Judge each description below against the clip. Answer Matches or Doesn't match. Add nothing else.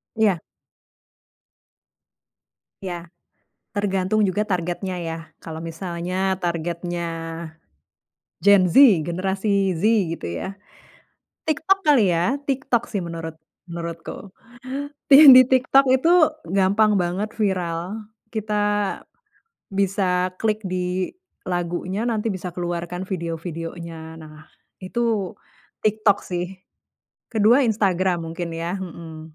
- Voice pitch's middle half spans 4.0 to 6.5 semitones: Doesn't match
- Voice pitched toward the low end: Doesn't match